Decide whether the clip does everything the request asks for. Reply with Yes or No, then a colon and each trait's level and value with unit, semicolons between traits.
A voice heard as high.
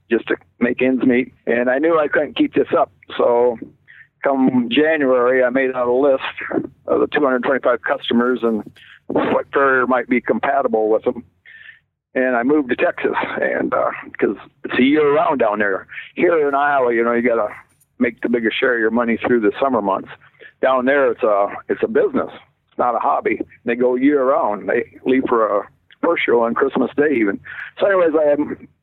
No: low, 130 Hz